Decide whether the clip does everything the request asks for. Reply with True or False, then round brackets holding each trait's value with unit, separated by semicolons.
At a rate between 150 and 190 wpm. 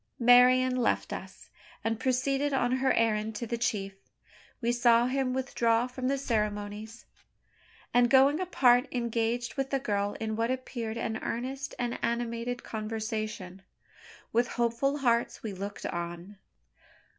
False (135 wpm)